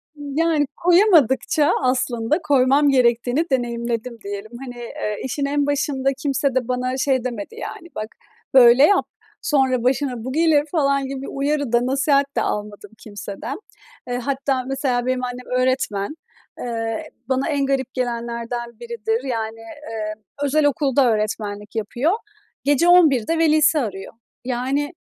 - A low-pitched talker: No, very high, 255 Hz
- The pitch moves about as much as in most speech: Yes, average, 3.2 semitones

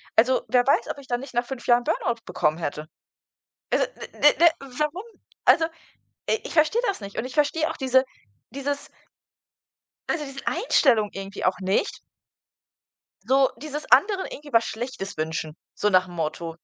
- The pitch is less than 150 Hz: No, very high, 255 Hz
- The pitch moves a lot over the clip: Yes, wide, 6.6 semitones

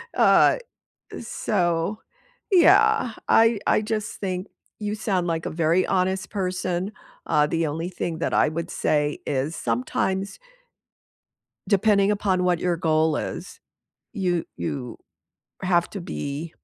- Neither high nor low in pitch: Yes, medium, 180 Hz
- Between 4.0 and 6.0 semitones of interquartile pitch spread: No, average, 3.5 semitones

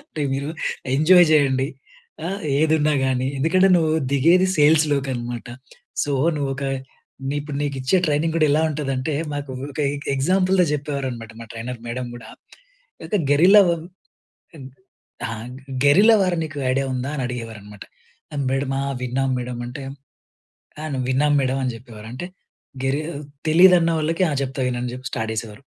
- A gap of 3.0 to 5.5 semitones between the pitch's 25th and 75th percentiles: Yes, average, 3.5 semitones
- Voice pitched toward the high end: No, medium, 140 Hz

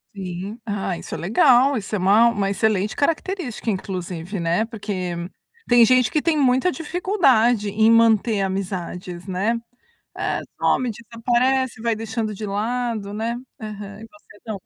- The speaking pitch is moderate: No, high, 220 Hz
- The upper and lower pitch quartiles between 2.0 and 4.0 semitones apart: Yes, average, 3.5 semitones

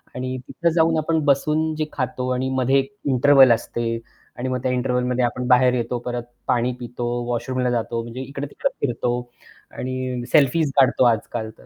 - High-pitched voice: No, low, 125 Hz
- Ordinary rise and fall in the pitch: No, narrow, 2.0 semitones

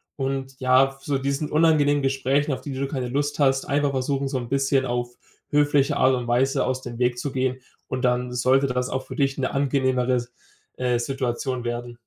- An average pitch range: No, narrow, 1.7 semitones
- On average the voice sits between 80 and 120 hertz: No, low, 130 Hz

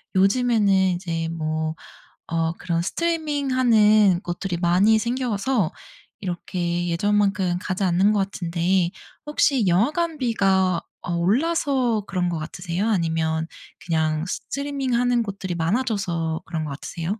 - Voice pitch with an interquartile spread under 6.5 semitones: Yes, average, 5.2 semitones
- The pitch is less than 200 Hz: Yes, high, 190 Hz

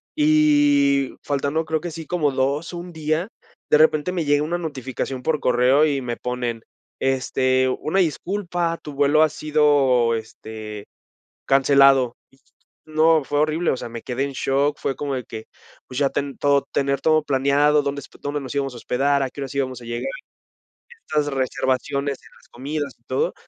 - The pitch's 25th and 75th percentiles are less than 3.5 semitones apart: Yes, average, 2.9 semitones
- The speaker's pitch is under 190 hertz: Yes, medium, 140 Hz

